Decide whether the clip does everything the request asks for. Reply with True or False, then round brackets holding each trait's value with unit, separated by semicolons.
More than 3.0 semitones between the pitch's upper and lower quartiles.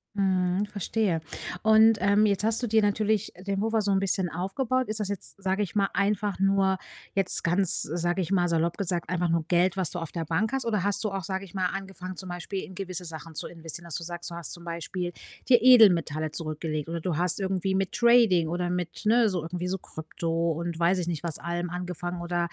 False (2.7 semitones)